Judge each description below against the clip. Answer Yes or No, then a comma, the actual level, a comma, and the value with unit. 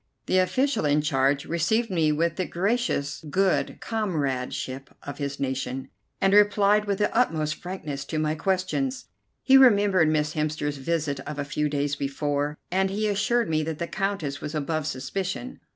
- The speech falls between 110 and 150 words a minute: No, average, 165 wpm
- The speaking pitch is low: No, medium, 160 Hz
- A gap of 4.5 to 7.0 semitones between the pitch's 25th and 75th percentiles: Yes, wide, 5.5 semitones